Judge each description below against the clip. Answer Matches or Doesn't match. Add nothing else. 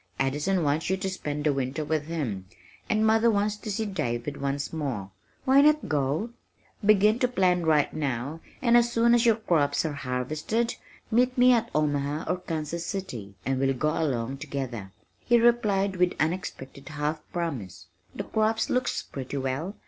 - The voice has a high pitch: Doesn't match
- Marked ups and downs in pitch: Matches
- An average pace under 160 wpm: Doesn't match